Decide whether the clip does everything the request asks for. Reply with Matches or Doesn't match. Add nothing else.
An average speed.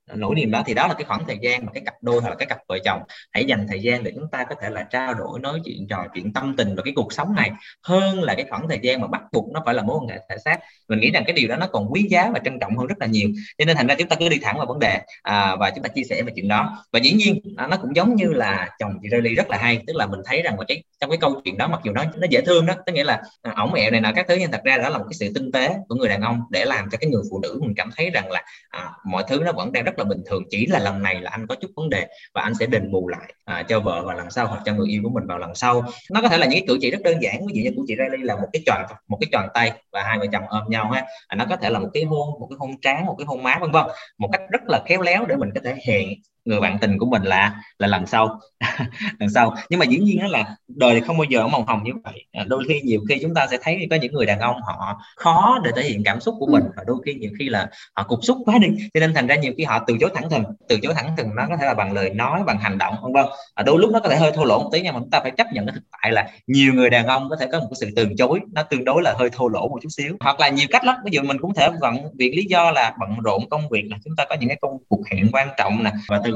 Doesn't match